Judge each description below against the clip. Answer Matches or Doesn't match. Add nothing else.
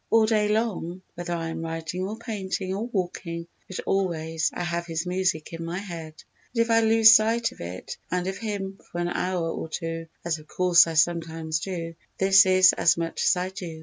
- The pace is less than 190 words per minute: Doesn't match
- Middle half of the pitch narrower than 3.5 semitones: Matches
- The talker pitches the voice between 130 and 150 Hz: Doesn't match